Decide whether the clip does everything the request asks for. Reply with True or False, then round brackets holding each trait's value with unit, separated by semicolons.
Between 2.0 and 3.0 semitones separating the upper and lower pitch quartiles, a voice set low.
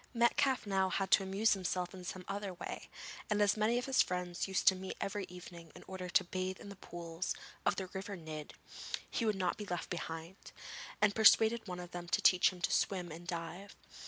False (2.4 semitones; 185 Hz)